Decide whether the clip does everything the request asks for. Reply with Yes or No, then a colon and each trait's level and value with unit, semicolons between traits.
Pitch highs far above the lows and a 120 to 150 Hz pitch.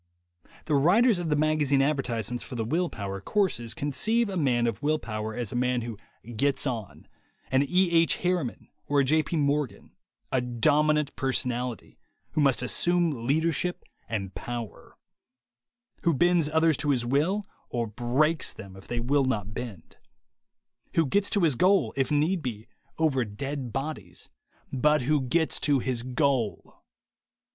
No: average, 4.7 semitones; medium, 140 Hz